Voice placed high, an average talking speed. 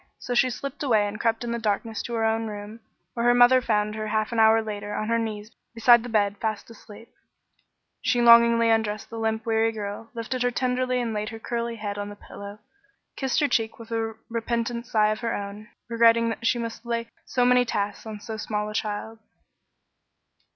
No: high, 225 Hz; fast, 215 wpm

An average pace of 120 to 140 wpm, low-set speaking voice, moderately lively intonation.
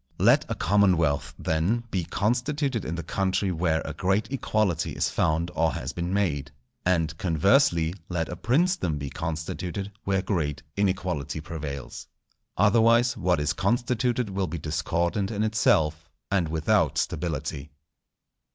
Yes: slow, 135 wpm; very low, 90 Hz; average, 4.4 semitones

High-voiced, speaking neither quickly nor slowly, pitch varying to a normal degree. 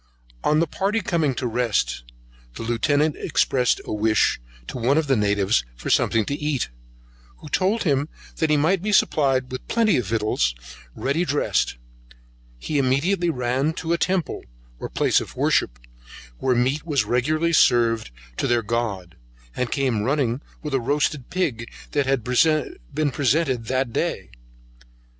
No: low, 135 Hz; average, 155 wpm; average, 4.7 semitones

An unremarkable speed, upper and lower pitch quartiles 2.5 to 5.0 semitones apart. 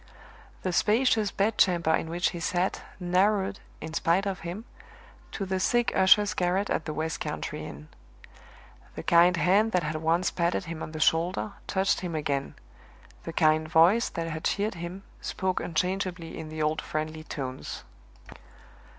Yes: average, 160 wpm; average, 3.2 semitones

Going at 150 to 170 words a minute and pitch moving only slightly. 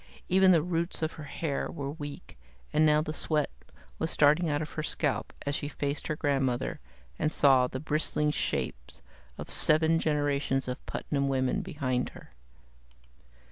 Yes: average, 160 wpm; narrow, 2.2 semitones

